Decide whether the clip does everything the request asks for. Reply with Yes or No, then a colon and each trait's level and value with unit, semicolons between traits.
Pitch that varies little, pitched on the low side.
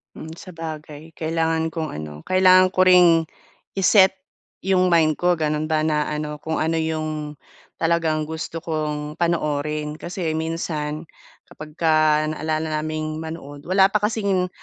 No: narrow, 1.9 semitones; medium, 160 Hz